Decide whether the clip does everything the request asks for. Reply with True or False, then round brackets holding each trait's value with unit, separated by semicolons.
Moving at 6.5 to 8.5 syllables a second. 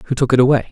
True (7.5 syllables/s)